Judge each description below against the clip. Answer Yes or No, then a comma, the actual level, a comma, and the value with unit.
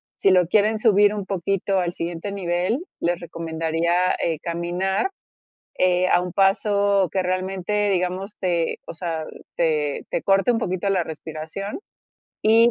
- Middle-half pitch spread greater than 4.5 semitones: No, average, 2.7 semitones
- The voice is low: No, medium, 185 Hz